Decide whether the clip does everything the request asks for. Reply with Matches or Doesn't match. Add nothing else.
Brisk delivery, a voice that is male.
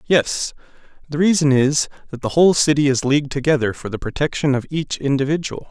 Doesn't match